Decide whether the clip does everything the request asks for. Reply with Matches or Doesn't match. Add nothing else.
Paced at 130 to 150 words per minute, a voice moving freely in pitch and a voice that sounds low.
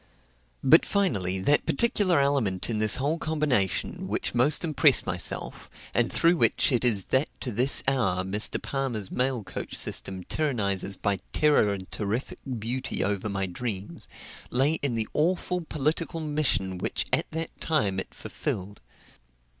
Matches